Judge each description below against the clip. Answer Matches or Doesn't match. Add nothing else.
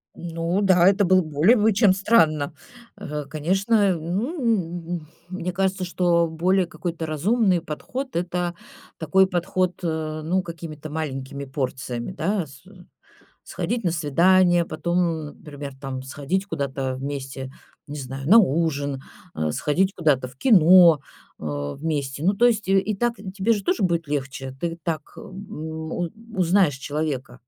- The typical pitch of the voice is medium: Matches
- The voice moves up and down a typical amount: Matches